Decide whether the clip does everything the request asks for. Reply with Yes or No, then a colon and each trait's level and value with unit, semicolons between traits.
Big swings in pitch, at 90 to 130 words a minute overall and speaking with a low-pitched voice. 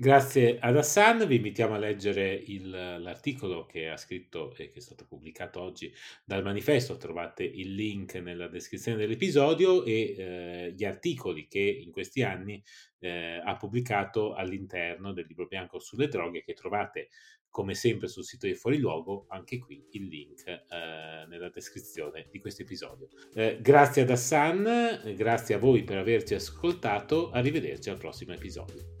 No: wide, 7.1 semitones; average, 155 wpm; low, 105 Hz